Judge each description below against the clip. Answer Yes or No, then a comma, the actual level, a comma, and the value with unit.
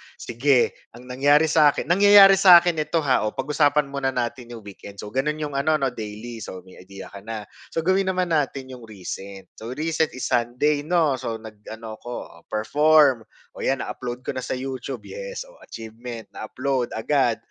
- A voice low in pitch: Yes, low, 130 Hz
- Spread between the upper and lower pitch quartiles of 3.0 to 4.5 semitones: No, average, 5.0 semitones